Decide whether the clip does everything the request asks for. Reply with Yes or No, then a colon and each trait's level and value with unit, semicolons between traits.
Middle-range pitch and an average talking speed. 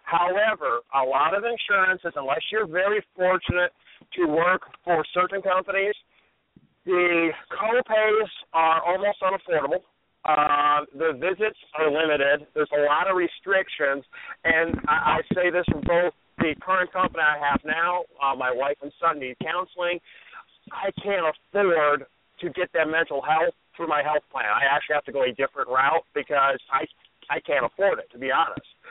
Yes: medium, 170 Hz; average, 160 wpm